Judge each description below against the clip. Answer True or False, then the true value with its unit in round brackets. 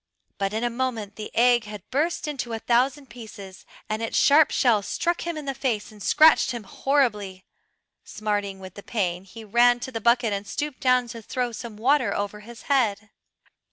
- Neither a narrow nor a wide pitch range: True (3.7 semitones)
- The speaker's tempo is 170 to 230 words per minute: True (190 wpm)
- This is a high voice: True (230 Hz)